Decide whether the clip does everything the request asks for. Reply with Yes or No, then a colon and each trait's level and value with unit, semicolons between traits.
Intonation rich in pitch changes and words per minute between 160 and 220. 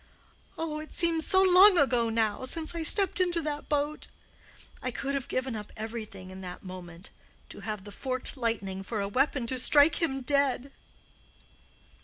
Yes: wide, 6.1 semitones; average, 170 wpm